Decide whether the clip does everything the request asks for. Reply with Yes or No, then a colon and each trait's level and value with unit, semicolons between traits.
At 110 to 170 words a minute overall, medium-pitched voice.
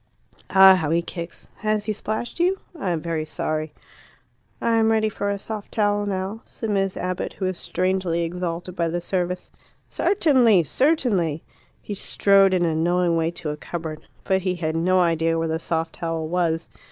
No: average, 180 wpm; medium, 180 Hz